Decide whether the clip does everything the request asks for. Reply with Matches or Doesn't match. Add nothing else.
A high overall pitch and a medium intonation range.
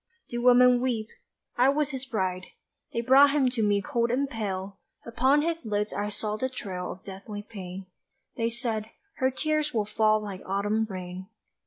Matches